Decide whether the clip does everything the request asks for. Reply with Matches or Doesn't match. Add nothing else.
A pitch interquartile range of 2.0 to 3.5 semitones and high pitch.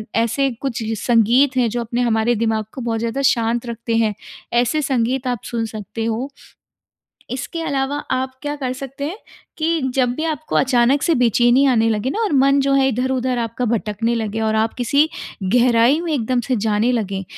Matches